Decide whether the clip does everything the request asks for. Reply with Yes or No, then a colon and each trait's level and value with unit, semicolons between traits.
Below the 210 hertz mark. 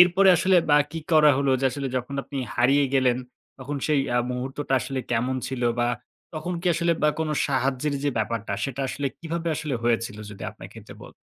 Yes: medium, 140 Hz